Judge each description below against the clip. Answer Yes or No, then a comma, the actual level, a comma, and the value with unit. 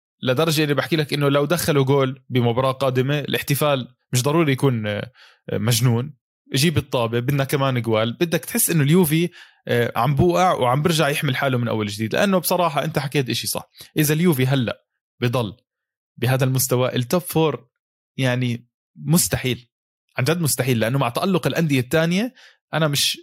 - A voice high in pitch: No, medium, 140 Hz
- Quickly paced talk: Yes, fast, 150 wpm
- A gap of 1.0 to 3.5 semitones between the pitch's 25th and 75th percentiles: No, average, 4.3 semitones